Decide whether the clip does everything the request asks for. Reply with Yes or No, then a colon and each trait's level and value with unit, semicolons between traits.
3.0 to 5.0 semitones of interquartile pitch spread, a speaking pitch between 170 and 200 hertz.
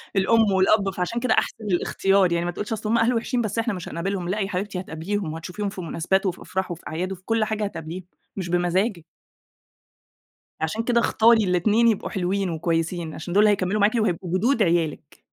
Yes: average, 3.5 semitones; high, 190 Hz